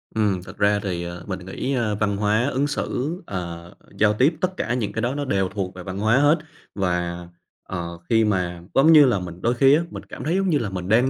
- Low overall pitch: Yes, low, 105 Hz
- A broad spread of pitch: Yes, wide, 6.2 semitones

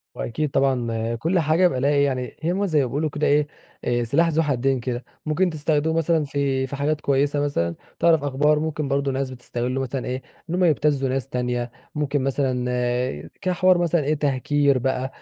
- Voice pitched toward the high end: No, medium, 140 Hz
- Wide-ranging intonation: No, average, 2.9 semitones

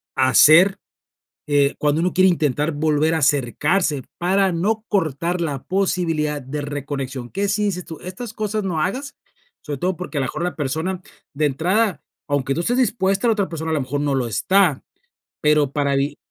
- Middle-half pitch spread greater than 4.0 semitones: Yes, average, 4.7 semitones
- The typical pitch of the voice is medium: Yes, medium, 160 Hz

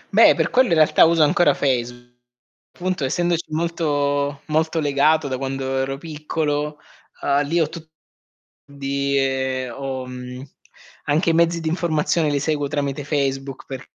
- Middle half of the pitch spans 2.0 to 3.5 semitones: Yes, average, 2.8 semitones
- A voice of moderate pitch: Yes, medium, 145 Hz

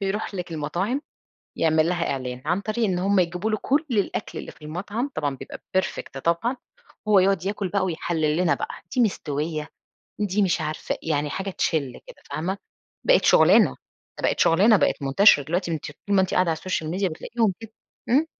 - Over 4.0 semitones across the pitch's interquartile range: Yes, average, 4.4 semitones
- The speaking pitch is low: No, medium, 180 Hz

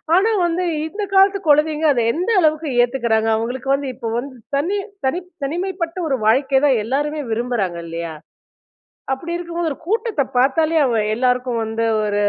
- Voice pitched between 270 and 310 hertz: Yes, very high, 275 Hz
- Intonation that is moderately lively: No, wide, 5.8 semitones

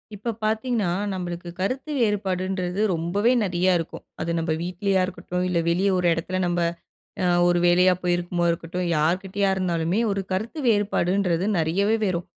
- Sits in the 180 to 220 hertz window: Yes, medium, 185 Hz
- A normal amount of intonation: No, narrow, 2.3 semitones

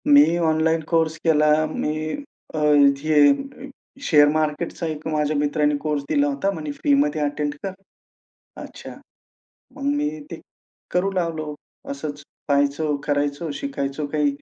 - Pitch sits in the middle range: Yes, medium, 155 Hz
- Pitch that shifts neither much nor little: No, narrow, 2.1 semitones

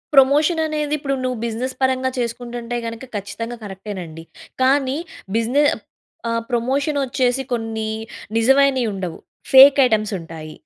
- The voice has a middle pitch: No, high, 245 Hz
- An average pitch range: Yes, average, 3.3 semitones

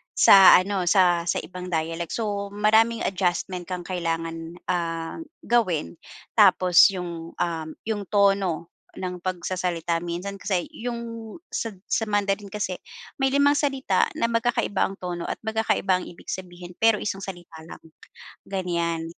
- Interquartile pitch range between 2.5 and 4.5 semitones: Yes, average, 3.1 semitones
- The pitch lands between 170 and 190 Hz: Yes, medium, 185 Hz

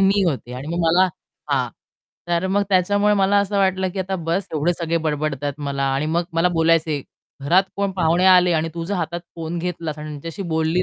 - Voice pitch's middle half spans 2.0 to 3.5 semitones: Yes, average, 3.0 semitones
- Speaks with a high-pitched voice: No, medium, 170 Hz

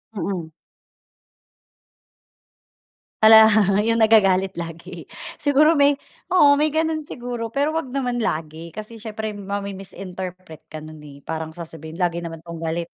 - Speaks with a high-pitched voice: Yes, high, 195 Hz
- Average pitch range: No, wide, 6.3 semitones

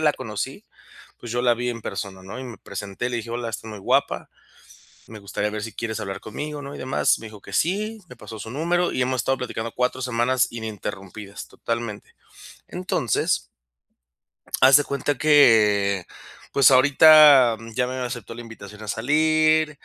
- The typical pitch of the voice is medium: No, low, 120 Hz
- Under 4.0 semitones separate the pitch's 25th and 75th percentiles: No, average, 4.3 semitones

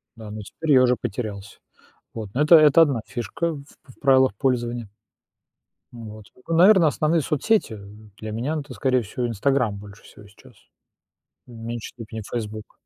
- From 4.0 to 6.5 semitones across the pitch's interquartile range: Yes, average, 4.7 semitones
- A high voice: No, low, 120 Hz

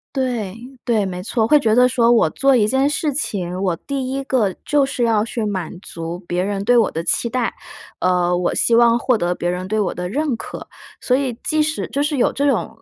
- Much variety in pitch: Yes, wide, 5.9 semitones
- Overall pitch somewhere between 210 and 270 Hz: Yes, high, 230 Hz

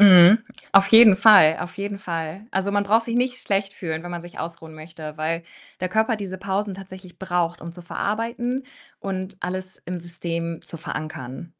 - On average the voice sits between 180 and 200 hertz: Yes, medium, 185 Hz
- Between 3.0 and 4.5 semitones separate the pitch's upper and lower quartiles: Yes, average, 3.3 semitones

